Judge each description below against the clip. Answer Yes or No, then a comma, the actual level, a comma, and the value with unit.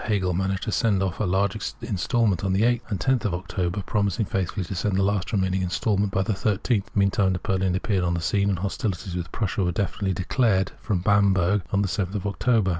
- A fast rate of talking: Yes, fast, 215 wpm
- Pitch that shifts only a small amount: Yes, narrow, 1.8 semitones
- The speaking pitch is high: No, very low, 95 Hz